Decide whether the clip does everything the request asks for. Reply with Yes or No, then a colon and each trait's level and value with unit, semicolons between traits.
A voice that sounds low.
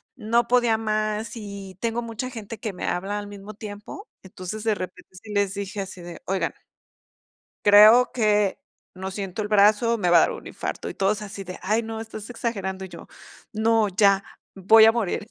No: high, 210 Hz